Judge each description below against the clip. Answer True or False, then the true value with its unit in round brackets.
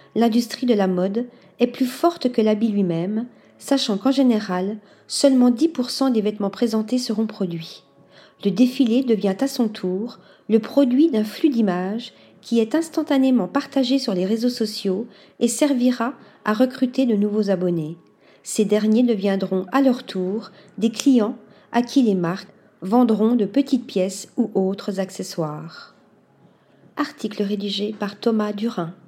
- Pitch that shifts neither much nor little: True (4.0 semitones)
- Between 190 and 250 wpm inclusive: False (145 wpm)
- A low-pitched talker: False (220 Hz)